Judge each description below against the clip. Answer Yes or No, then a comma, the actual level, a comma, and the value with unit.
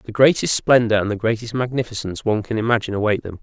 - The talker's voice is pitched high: No, low, 110 Hz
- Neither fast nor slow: No, fast, 210 wpm